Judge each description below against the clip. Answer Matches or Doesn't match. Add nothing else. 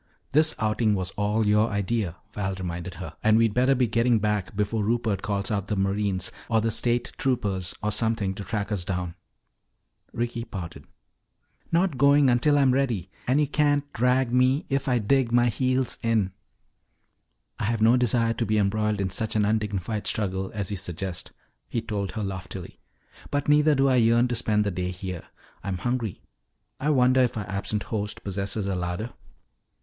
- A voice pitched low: Matches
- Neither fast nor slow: Matches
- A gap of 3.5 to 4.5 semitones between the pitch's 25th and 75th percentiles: Matches